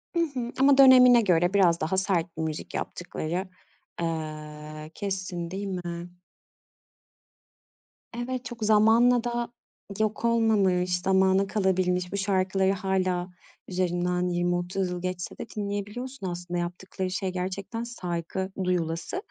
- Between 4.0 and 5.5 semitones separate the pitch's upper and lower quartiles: No, average, 2.9 semitones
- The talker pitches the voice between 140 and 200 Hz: Yes, medium, 185 Hz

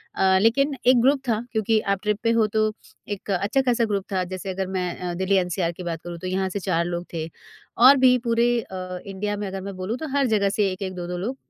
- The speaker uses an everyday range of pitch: Yes, average, 3.6 semitones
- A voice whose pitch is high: Yes, high, 195 Hz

